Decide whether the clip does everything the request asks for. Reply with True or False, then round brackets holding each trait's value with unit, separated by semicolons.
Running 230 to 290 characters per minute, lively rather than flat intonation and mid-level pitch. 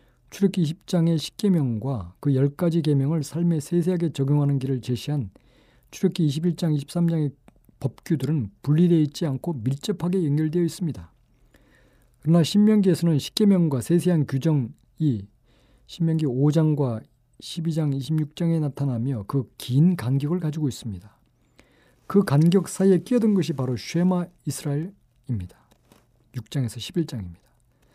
False (285 characters per minute; 4.6 semitones; 150 Hz)